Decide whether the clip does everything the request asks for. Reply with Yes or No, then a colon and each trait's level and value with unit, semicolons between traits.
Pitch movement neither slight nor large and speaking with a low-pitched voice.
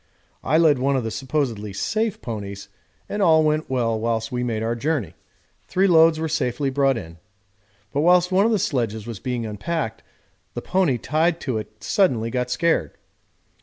No: wide, 6.2 semitones; low, 130 Hz